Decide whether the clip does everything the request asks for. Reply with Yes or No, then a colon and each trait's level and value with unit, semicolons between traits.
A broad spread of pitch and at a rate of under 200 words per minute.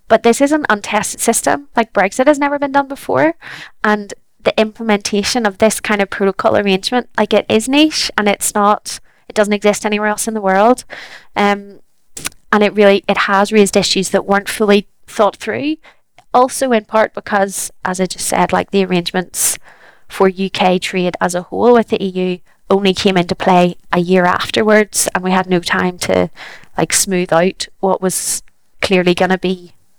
No: average, 2.7 semitones; average, 185 wpm